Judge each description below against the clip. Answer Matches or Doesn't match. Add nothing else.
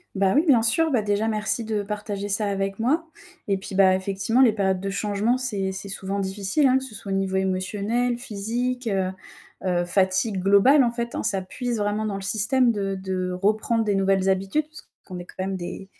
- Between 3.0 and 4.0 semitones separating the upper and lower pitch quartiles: Matches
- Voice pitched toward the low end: Doesn't match